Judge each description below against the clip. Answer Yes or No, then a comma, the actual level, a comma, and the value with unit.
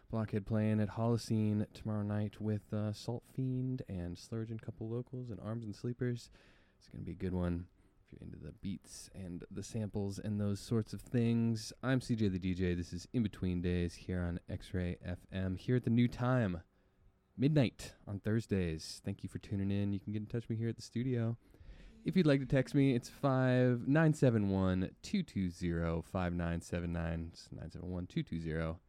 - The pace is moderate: Yes, average, 180 wpm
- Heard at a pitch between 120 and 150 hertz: No, low, 105 Hz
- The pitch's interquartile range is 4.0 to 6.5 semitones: Yes, average, 4.6 semitones